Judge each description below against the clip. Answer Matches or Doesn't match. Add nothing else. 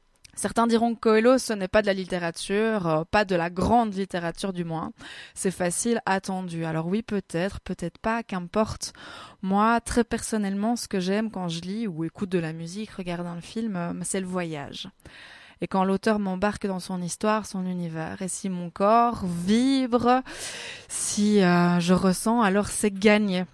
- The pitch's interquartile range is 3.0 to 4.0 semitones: Matches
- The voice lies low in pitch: Doesn't match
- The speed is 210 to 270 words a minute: Doesn't match